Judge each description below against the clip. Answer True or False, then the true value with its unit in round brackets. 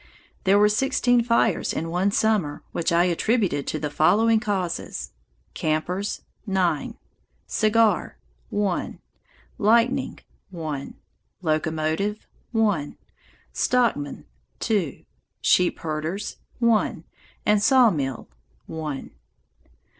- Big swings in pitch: True (5.8 semitones)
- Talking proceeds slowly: True (90 wpm)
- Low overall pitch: False (190 Hz)